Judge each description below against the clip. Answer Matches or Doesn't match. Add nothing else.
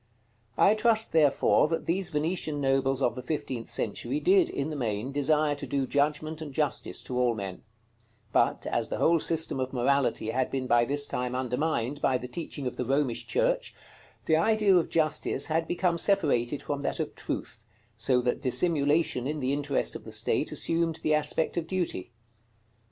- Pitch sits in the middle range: Matches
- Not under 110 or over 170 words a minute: Doesn't match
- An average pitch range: Matches